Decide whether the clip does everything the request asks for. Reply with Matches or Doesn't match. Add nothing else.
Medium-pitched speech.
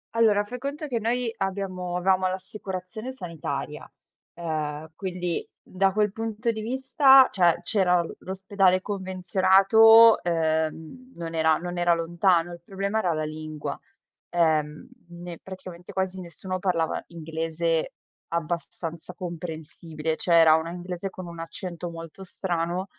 Matches